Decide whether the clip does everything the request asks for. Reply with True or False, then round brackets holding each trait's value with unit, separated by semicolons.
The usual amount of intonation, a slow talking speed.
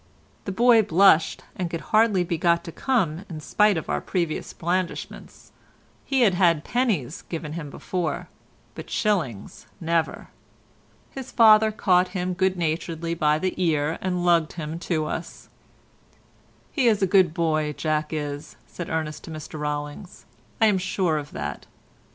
False (3.5 semitones; 150 wpm)